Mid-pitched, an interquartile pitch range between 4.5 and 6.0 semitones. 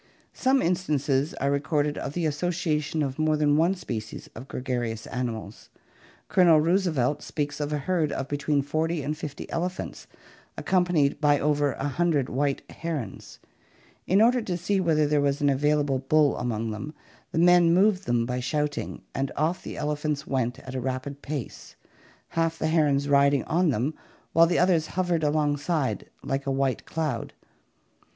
No: medium, 150 Hz; average, 3.2 semitones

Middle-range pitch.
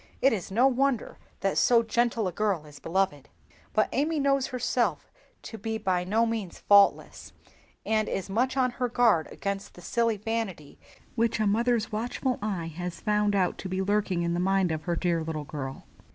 No: high, 210 Hz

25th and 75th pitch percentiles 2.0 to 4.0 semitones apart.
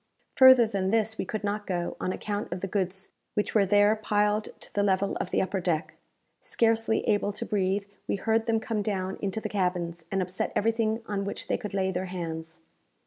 Yes: narrow, 2.5 semitones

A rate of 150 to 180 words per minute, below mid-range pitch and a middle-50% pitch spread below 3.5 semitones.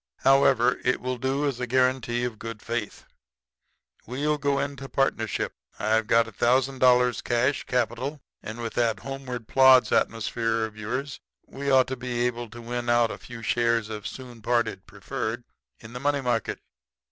Yes: average, 170 wpm; low, 120 Hz; narrow, 2.4 semitones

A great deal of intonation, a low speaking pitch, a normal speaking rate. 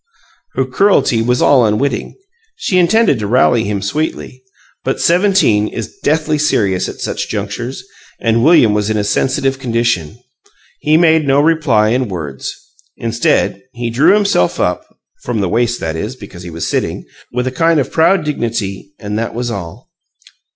Yes: wide, 6.3 semitones; low, 120 Hz; average, 165 wpm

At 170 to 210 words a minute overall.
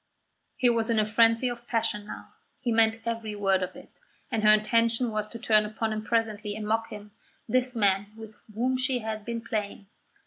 Yes: average, 200 wpm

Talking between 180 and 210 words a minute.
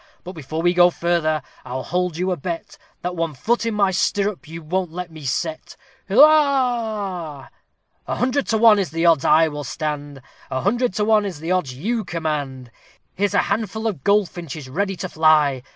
Yes: average, 185 wpm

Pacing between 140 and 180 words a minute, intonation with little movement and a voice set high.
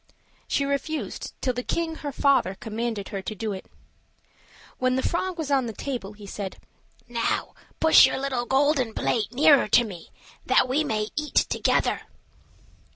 No: average, 160 wpm; average, 4.6 semitones; very high, 255 Hz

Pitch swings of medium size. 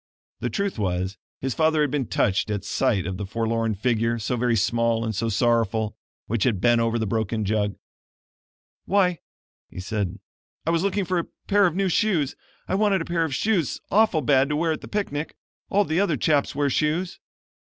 No: wide, 7.2 semitones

